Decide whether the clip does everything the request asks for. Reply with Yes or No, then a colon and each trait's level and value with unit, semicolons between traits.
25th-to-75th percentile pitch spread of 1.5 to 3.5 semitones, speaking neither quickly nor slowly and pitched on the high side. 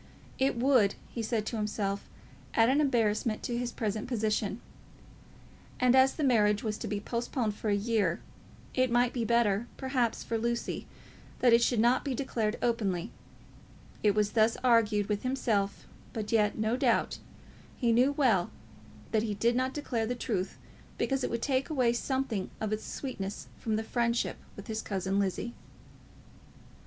Yes: average, 2.8 semitones; average, 170 wpm; high, 230 Hz